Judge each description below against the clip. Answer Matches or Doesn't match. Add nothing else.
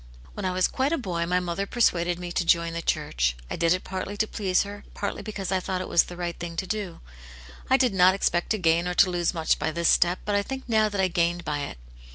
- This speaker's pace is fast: Matches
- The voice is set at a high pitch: Doesn't match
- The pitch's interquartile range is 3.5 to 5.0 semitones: Doesn't match